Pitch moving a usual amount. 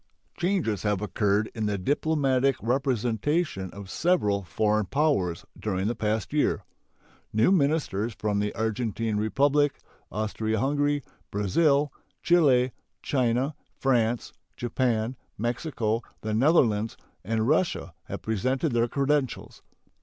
Yes: average, 4.9 semitones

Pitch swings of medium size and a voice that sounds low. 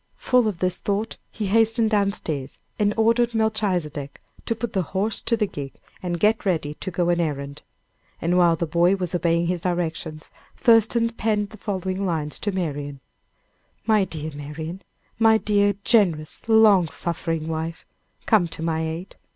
No: average, 4.8 semitones; medium, 180 Hz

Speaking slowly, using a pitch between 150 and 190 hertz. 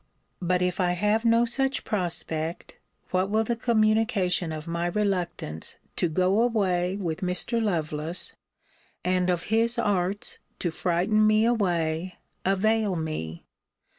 Yes: slow, 130 wpm; medium, 185 Hz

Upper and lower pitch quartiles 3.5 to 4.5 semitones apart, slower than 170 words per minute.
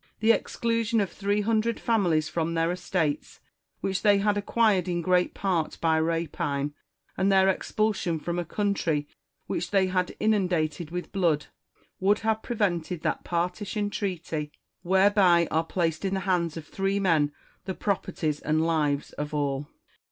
Yes: average, 3.8 semitones; average, 150 wpm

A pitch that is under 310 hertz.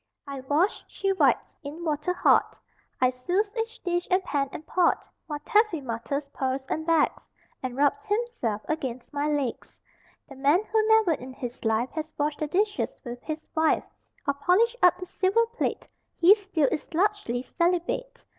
No: very high, 315 Hz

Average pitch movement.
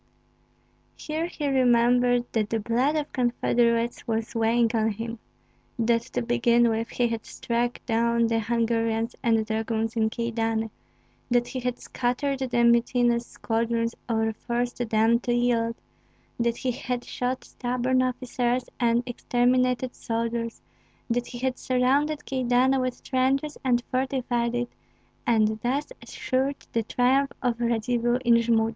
No: narrow, 1.6 semitones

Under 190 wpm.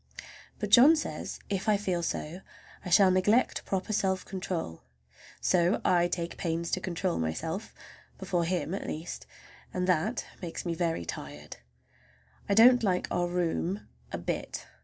Yes: average, 140 wpm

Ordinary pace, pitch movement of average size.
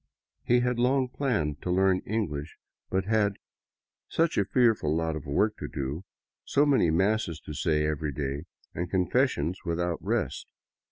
No: average, 165 wpm; wide, 6.3 semitones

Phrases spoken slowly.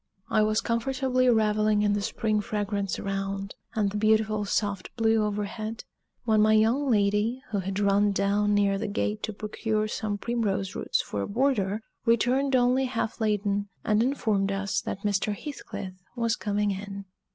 No: average, 165 wpm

